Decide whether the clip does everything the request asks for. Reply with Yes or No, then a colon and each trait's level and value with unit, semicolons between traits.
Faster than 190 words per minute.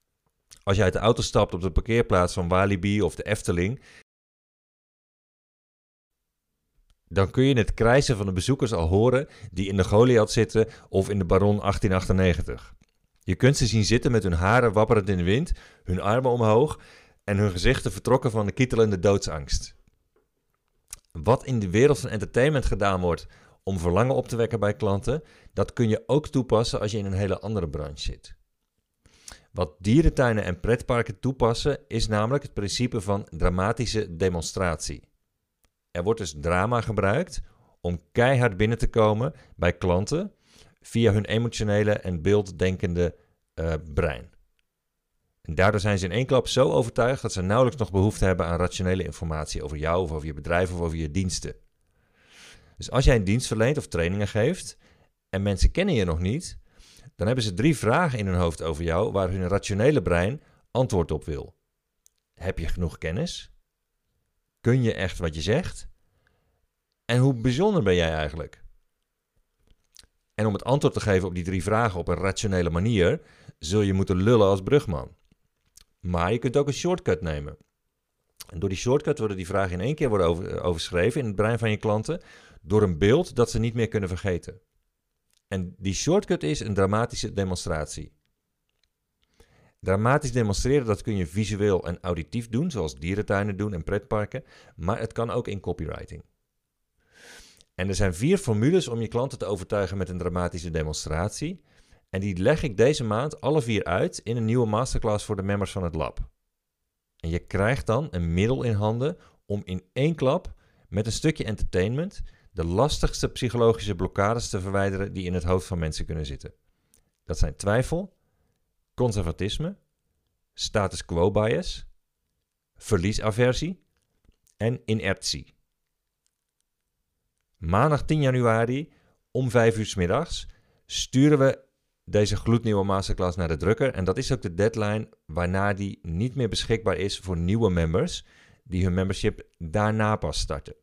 No: average, 165 wpm